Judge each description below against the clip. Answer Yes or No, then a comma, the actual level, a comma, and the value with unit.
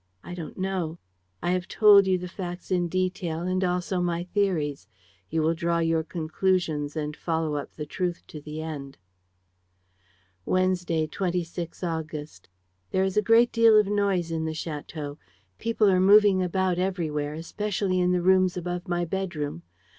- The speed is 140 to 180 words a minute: Yes, average, 160 wpm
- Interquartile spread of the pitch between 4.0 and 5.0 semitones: No, average, 2.8 semitones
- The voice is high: No, medium, 175 Hz